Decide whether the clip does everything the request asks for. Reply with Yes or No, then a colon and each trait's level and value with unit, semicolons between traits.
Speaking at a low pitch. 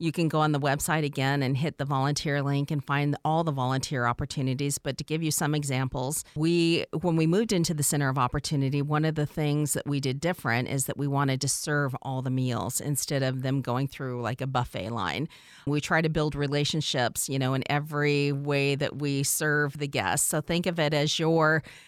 No: medium, 145 Hz